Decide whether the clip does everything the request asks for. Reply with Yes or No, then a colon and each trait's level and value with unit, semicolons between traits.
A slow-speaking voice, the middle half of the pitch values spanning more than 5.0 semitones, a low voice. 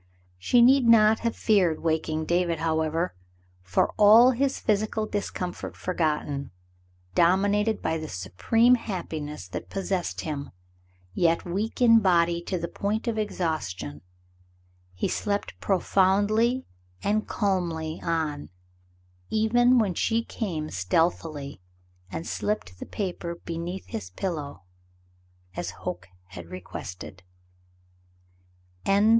No: slow, 110 wpm; wide, 5.4 semitones; medium, 175 Hz